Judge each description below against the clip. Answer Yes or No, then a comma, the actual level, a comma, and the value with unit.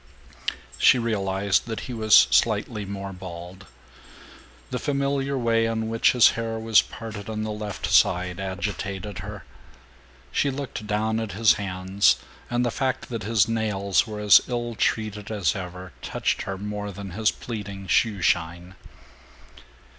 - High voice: No, low, 105 Hz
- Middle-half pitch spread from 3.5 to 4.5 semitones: No, average, 2.7 semitones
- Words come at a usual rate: Yes, average, 145 wpm